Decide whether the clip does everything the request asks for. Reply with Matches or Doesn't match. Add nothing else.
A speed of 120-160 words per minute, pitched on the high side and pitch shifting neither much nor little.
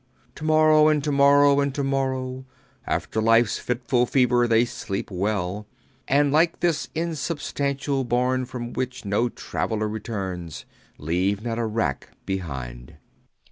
Doesn't match